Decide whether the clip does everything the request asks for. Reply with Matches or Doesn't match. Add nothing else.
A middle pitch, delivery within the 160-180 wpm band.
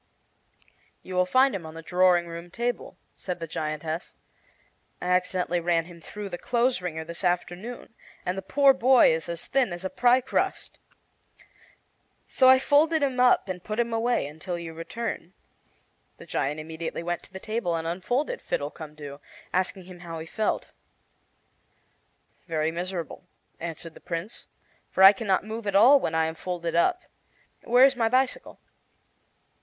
Matches